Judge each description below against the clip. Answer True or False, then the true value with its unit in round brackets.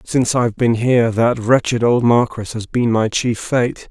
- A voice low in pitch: True (115 Hz)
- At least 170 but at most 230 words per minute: True (200 wpm)